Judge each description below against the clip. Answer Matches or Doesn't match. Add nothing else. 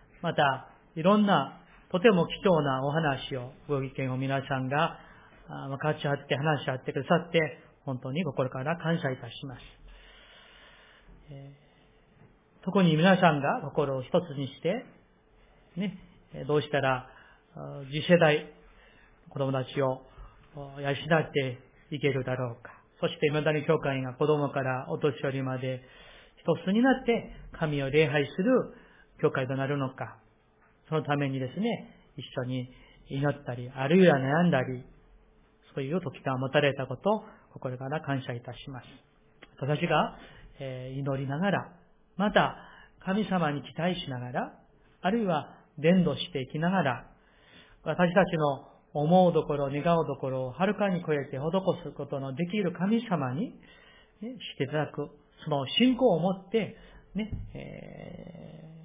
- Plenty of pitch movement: Doesn't match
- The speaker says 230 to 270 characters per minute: Matches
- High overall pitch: Doesn't match